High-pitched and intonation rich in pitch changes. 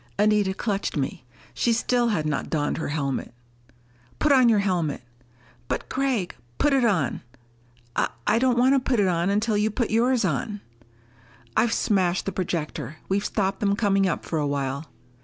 Yes: high, 200 Hz; wide, 6.1 semitones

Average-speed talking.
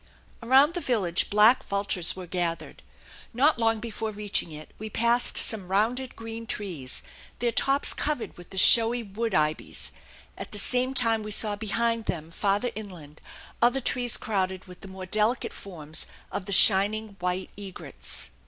Yes: average, 160 wpm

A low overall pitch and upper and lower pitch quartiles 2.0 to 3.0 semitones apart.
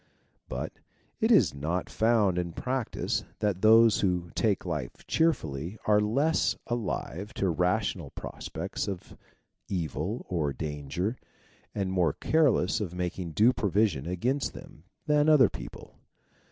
No: very low, 95 Hz; average, 5.2 semitones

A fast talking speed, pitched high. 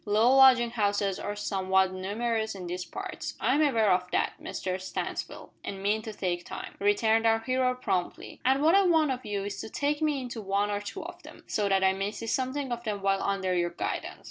Yes: fast, 220 wpm; high, 210 Hz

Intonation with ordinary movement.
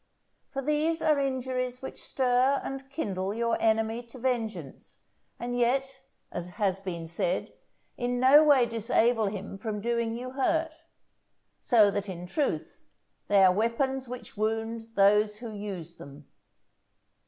Yes: average, 4.3 semitones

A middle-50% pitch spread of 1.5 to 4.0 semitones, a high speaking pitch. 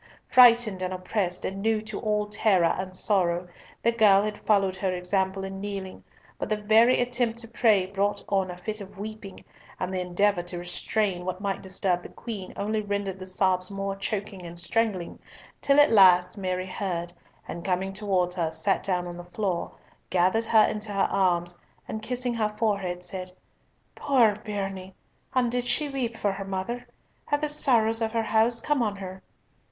Yes: average, 3.1 semitones; high, 200 Hz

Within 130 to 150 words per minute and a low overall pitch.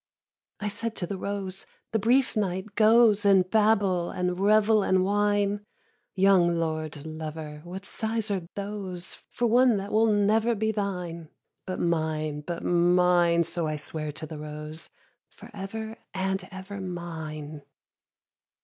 No: average, 145 wpm; high, 190 Hz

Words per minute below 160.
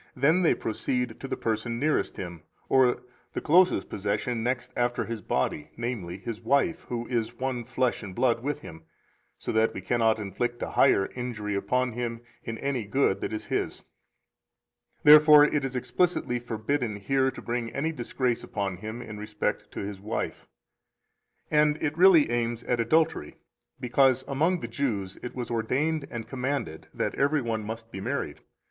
No: average, 170 wpm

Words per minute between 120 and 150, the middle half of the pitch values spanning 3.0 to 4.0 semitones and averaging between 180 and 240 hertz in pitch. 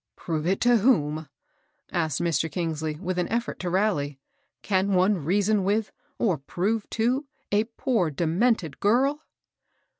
No: average, 140 wpm; average, 5.3 semitones; high, 190 Hz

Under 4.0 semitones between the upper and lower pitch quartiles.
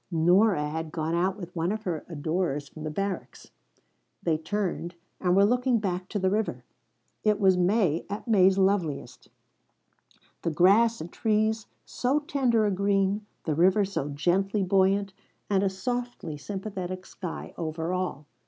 Yes: average, 3.4 semitones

